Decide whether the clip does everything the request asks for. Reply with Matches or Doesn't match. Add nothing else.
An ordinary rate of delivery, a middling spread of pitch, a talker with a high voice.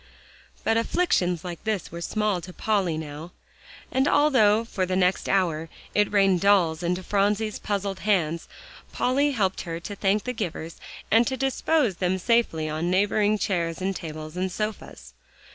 Matches